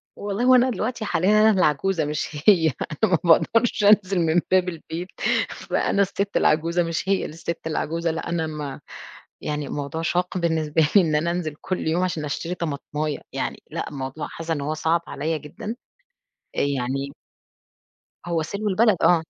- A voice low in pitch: No, medium, 165 Hz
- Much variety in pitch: No, average, 3.6 semitones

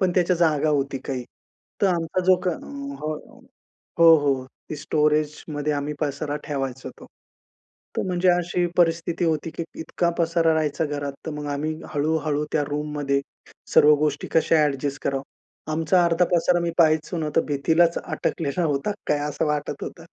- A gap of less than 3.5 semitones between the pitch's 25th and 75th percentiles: Yes, narrow, 2.6 semitones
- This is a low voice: No, medium, 155 Hz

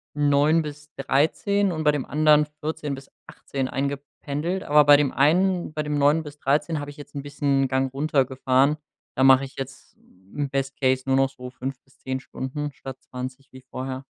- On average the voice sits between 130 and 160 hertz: Yes, medium, 140 Hz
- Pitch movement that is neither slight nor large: No, narrow, 2.0 semitones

